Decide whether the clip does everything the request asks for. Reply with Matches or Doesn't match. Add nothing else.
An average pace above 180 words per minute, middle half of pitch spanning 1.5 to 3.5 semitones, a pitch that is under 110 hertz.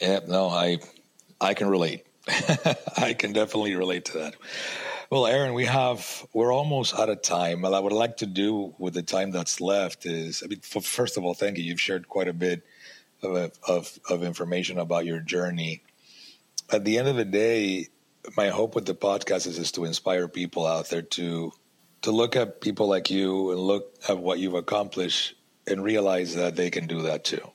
Matches